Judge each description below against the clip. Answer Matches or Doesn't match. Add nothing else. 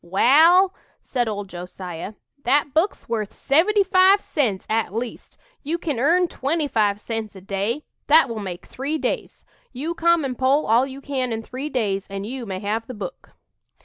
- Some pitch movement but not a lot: Doesn't match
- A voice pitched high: Matches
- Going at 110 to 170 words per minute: Doesn't match